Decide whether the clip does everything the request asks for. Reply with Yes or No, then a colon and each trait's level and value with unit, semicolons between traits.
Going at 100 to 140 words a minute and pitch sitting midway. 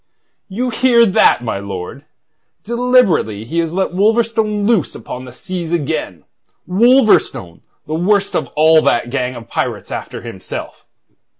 Yes: slow, 135 wpm; medium, 175 Hz